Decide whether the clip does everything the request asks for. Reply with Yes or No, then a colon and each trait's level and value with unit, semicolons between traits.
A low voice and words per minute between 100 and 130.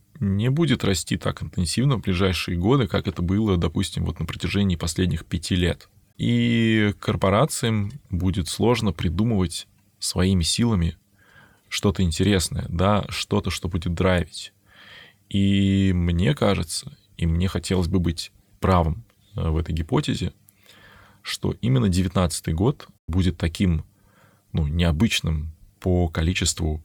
Yes: very low, 95 Hz; average, 120 wpm